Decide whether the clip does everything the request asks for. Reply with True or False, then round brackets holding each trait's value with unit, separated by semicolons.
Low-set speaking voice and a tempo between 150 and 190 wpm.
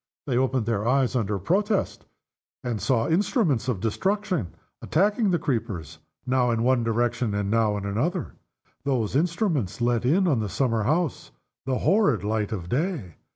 True (125 Hz; 155 wpm)